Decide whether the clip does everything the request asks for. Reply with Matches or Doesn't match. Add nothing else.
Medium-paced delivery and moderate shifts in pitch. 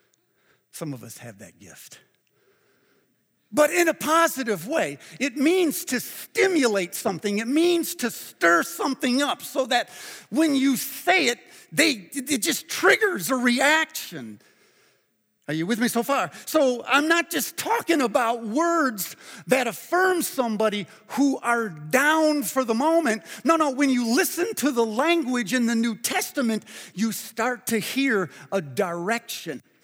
Doesn't match